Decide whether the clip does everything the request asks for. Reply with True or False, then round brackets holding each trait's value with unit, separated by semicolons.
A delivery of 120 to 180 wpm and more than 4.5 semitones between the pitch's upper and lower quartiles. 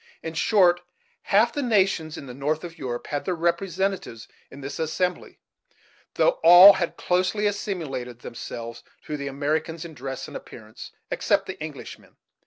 True (160 wpm; 5.1 semitones)